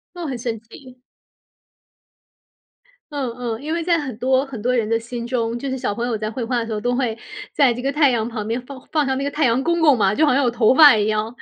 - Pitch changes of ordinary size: Yes, average, 3.3 semitones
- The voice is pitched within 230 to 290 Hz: Yes, very high, 250 Hz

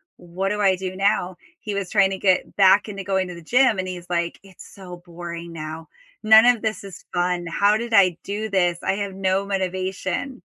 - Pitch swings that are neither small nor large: No, narrow, 2.3 semitones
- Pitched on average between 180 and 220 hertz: Yes, high, 190 Hz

